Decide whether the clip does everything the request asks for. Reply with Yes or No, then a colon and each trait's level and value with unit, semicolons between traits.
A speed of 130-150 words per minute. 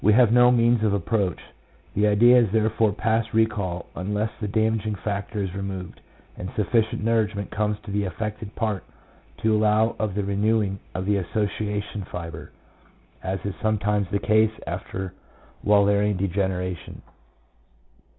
Yes: average, 140 wpm